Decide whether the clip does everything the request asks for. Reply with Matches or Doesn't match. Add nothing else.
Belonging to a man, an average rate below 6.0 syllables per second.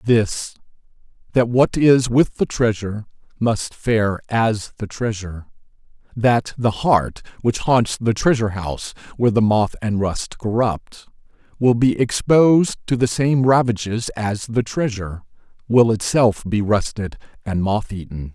Matches